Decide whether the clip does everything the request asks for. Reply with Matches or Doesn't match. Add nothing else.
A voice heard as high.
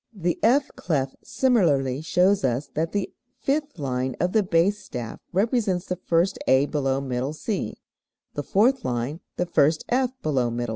Doesn't match